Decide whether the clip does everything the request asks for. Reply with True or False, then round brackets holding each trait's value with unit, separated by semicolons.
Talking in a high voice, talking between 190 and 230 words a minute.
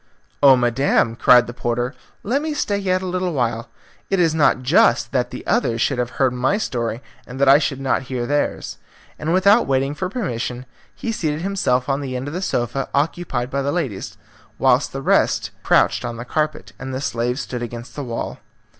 False (135 Hz; 200 wpm)